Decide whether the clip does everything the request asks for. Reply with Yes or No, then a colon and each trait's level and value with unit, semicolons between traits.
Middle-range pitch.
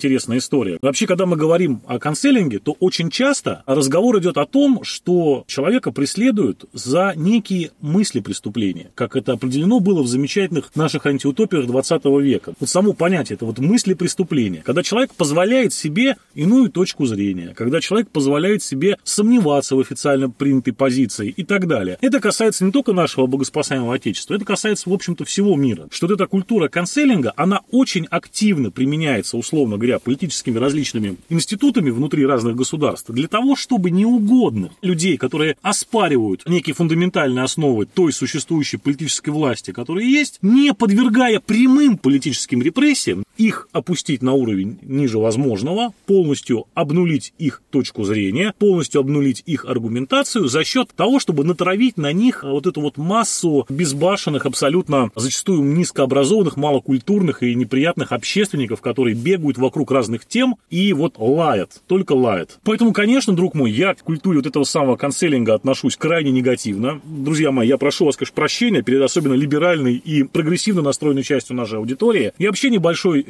Yes: medium, 155 Hz